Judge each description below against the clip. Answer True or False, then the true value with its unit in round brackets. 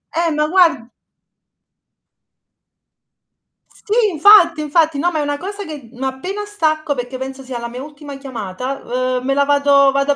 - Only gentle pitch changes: False (3.6 semitones)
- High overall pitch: True (285 Hz)